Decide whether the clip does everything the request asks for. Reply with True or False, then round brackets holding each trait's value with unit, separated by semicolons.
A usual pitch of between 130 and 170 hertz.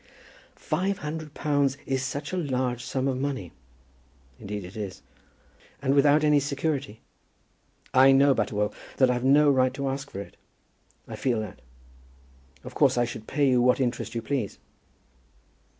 True (135 Hz)